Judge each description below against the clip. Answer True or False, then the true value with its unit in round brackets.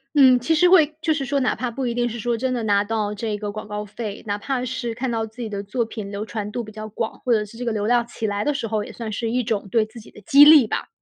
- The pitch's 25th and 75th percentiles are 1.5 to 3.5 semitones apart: True (3.0 semitones)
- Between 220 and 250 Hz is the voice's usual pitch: True (230 Hz)